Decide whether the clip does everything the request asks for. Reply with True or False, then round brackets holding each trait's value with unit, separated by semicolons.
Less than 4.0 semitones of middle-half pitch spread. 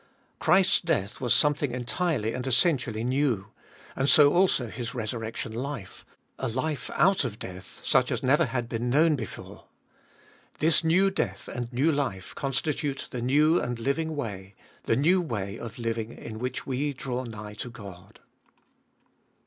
False (4.5 semitones)